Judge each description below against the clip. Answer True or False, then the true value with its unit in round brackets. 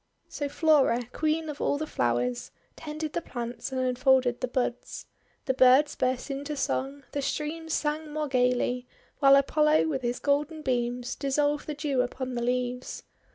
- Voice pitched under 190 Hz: False (275 Hz)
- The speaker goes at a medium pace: True (160 wpm)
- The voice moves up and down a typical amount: True (3.2 semitones)